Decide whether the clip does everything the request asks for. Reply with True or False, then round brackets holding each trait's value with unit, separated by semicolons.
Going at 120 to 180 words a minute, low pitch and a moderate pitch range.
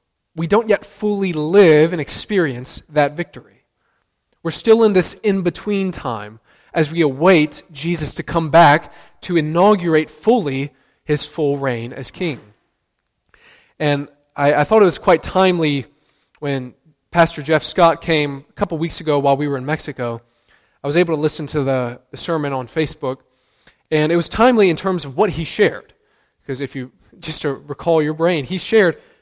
False (175 wpm; 155 Hz; 3.7 semitones)